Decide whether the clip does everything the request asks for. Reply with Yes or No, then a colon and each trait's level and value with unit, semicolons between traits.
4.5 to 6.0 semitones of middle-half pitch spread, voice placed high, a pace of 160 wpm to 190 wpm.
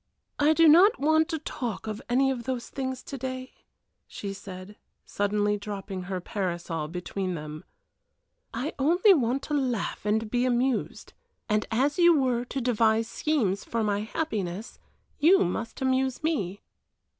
No: average, 5.1 semitones; high, 235 Hz; average, 150 wpm